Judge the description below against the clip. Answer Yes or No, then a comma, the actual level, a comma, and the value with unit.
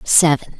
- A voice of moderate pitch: Yes, medium, 145 Hz